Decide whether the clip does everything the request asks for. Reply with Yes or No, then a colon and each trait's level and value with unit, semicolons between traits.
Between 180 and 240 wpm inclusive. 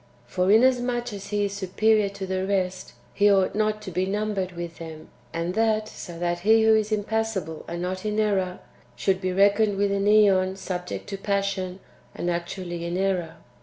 Yes: average, 185 wpm